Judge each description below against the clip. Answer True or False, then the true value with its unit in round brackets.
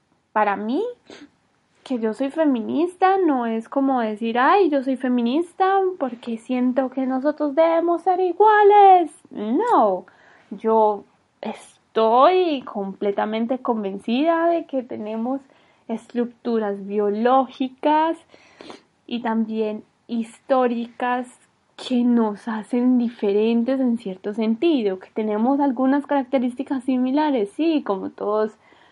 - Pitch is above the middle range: True (255 Hz)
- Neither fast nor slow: False (100 wpm)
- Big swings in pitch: False (5.0 semitones)